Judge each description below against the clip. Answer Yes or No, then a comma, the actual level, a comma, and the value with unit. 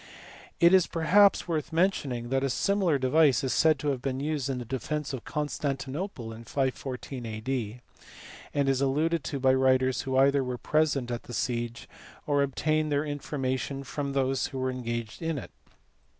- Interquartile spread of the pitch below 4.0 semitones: Yes, average, 2.8 semitones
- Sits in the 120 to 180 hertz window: Yes, low, 135 Hz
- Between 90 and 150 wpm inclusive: No, average, 180 wpm